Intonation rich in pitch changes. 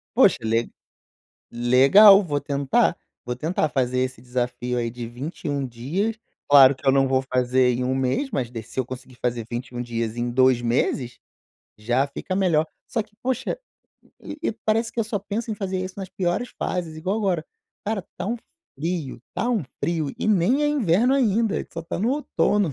Yes: wide, 8.3 semitones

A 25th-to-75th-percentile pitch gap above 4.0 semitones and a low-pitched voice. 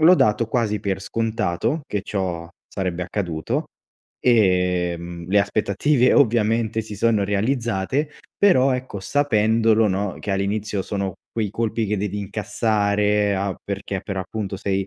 No: average, 2.8 semitones; low, 105 Hz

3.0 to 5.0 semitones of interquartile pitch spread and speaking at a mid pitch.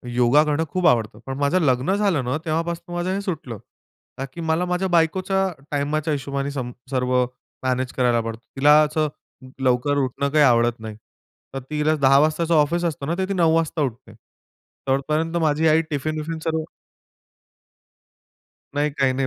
Yes: average, 3.6 semitones; medium, 150 Hz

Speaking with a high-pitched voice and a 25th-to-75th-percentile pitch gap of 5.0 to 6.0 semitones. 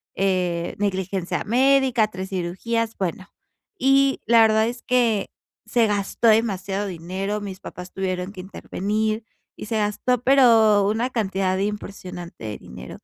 No: high, 205 Hz; average, 3.3 semitones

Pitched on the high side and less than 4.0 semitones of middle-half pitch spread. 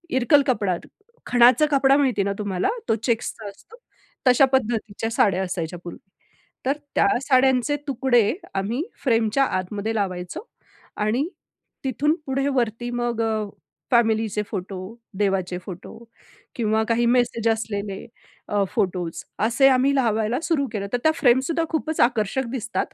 No: high, 230 Hz; average, 4.3 semitones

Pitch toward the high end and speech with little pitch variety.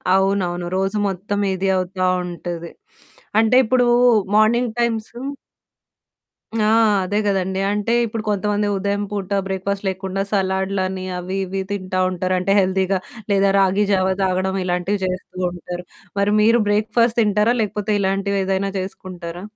Yes: high, 195 Hz; narrow, 1.8 semitones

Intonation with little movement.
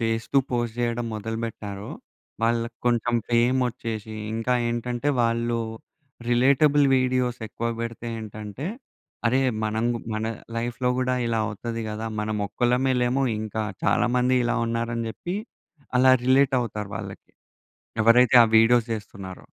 Yes: narrow, 1.8 semitones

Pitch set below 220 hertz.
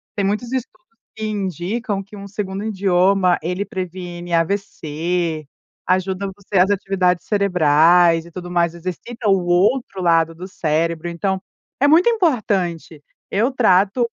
Yes: medium, 185 Hz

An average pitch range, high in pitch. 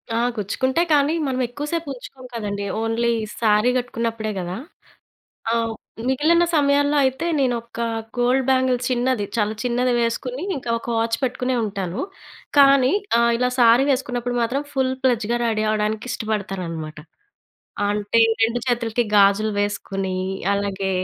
Yes: average, 3.5 semitones; high, 235 Hz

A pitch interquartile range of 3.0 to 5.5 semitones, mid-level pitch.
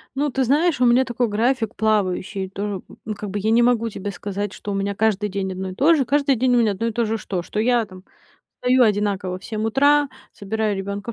No: average, 3.6 semitones; high, 220 Hz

